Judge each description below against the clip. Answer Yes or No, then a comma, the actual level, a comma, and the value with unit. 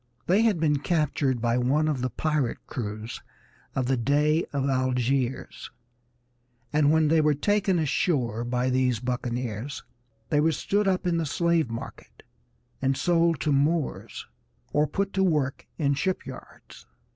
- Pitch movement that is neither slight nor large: Yes, average, 4.3 semitones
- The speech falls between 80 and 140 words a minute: No, average, 150 wpm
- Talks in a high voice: No, medium, 145 Hz